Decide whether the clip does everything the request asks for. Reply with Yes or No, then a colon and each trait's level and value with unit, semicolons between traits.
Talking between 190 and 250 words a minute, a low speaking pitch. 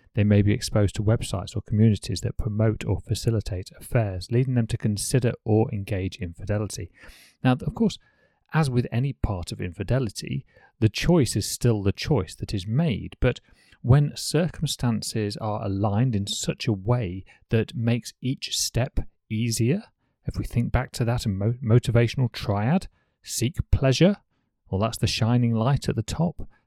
No: average, 155 wpm; low, 115 Hz